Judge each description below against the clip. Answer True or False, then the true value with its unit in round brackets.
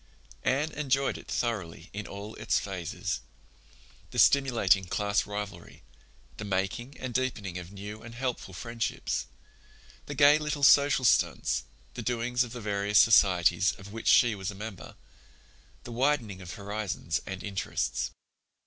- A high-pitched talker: False (110 Hz)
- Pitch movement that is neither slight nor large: True (4.2 semitones)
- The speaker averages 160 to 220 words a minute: False (140 wpm)